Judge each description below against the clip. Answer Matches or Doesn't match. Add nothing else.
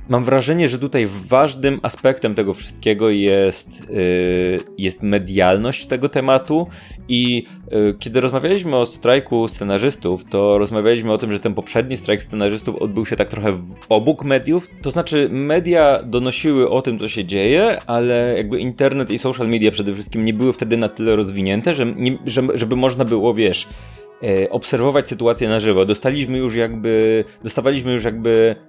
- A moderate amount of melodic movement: Matches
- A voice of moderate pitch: Doesn't match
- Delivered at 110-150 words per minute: Doesn't match